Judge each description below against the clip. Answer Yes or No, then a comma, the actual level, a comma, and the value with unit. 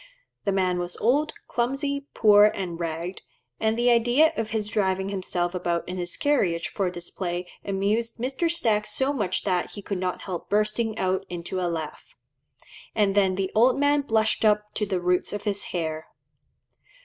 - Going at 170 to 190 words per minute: Yes, average, 175 wpm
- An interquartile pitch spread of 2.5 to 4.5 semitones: Yes, average, 4.0 semitones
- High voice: Yes, high, 200 Hz